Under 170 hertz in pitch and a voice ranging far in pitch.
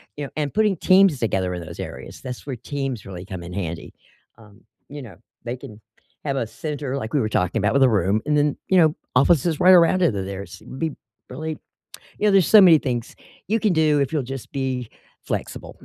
Yes: low, 135 Hz; wide, 6.4 semitones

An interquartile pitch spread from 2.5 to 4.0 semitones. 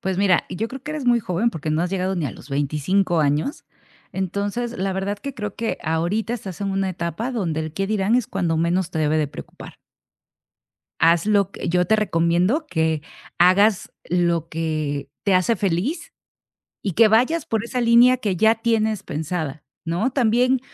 No: average, 5.2 semitones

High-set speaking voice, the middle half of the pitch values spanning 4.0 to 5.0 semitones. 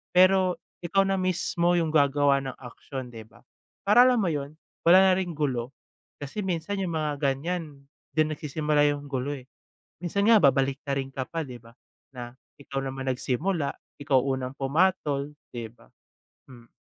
No: medium, 145 Hz; average, 4.6 semitones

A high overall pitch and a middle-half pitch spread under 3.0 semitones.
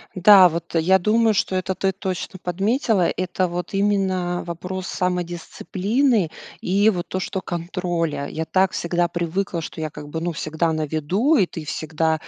No: medium, 180 Hz; narrow, 2.4 semitones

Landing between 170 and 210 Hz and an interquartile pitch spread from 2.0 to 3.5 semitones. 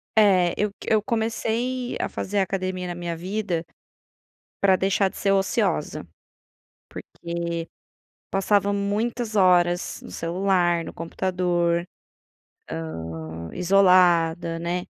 Yes: medium, 185 Hz; average, 2.8 semitones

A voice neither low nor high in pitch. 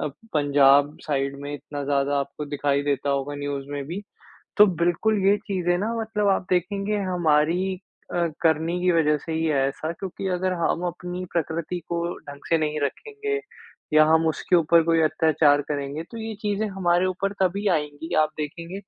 Yes: medium, 165 Hz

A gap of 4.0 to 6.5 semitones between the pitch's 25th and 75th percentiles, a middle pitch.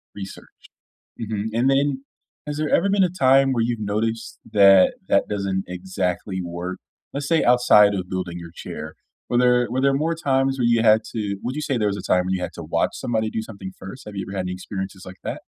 No: wide, 5.6 semitones; low, 110 Hz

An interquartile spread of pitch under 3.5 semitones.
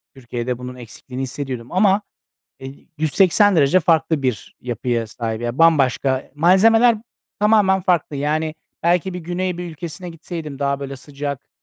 No: wide, 5.4 semitones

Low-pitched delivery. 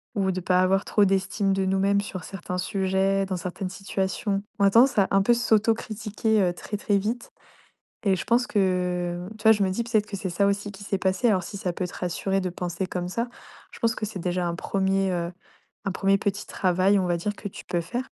No: high, 195 Hz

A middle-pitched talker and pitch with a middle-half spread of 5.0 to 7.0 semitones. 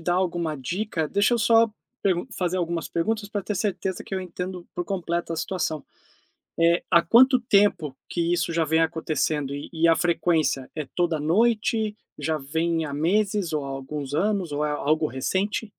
No: medium, 170 Hz; average, 4.0 semitones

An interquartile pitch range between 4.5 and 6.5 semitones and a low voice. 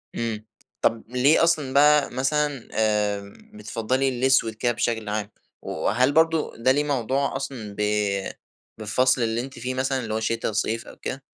No: average, 3.5 semitones; low, 125 Hz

